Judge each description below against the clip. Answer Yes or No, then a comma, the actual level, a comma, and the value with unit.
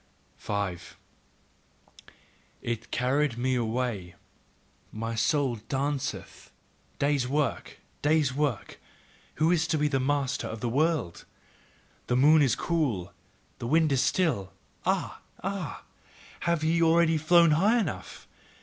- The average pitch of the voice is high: No, medium, 140 Hz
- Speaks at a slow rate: Yes, slow, 115 wpm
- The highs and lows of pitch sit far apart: No, average, 4.8 semitones